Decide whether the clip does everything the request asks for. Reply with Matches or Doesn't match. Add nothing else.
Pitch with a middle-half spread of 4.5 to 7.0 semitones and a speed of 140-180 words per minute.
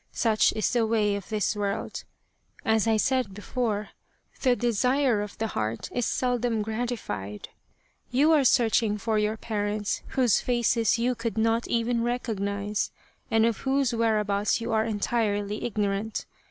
Doesn't match